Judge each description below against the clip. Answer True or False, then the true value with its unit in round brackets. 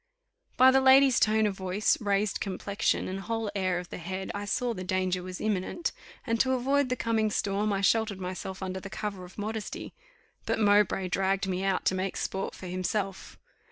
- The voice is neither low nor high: False (200 Hz)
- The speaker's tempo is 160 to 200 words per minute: True (195 wpm)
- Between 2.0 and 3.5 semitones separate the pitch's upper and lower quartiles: True (2.8 semitones)